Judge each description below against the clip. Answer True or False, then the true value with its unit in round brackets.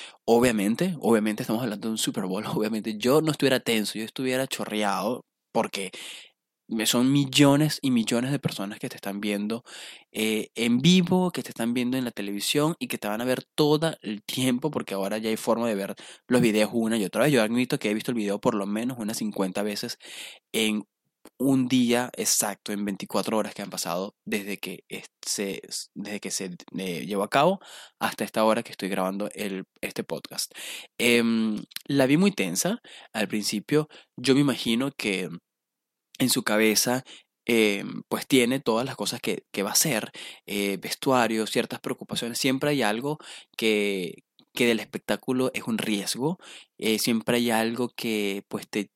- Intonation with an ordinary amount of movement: True (3.8 semitones)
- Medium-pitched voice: False (115 Hz)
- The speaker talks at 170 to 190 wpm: True (180 wpm)